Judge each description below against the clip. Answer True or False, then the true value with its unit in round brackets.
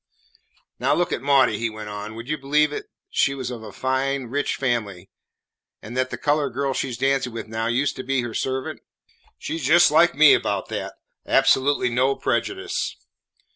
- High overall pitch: False (130 Hz)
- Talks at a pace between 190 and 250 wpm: True (195 wpm)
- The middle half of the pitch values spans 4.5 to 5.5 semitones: False (3.5 semitones)